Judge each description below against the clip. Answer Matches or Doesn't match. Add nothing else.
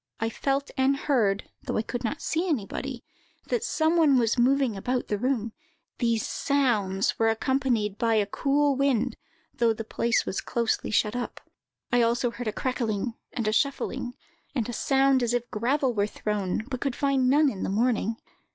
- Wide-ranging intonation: Doesn't match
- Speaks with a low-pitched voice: Doesn't match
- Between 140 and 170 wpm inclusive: Doesn't match